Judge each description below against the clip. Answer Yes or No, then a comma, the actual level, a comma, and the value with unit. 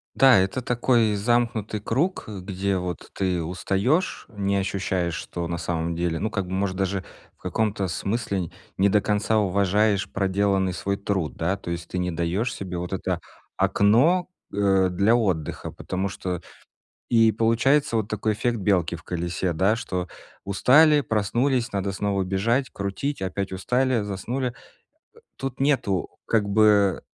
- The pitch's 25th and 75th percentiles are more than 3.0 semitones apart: Yes, average, 3.5 semitones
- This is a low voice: Yes, low, 100 Hz